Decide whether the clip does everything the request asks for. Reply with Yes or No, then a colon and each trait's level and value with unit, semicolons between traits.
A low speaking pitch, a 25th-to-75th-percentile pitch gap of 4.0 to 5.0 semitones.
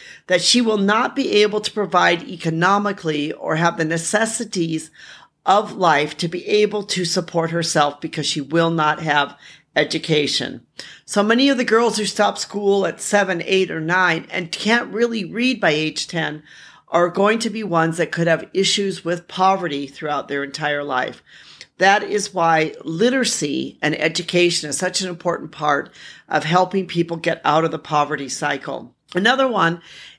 No: medium, 175 Hz; average, 4.5 semitones